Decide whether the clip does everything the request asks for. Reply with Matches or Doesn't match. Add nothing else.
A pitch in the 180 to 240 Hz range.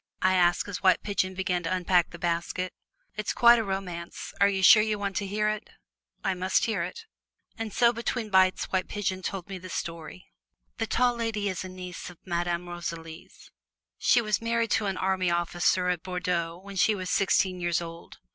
Matches